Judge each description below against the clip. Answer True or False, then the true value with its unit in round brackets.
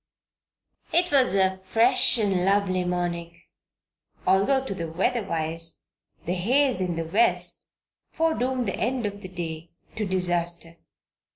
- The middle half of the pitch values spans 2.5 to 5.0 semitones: False (5.5 semitones)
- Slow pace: True (130 wpm)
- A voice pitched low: False (190 Hz)